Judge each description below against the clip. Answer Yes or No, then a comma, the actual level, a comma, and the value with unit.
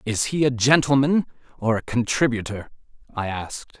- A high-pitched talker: No, low, 125 Hz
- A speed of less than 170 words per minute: Yes, average, 140 wpm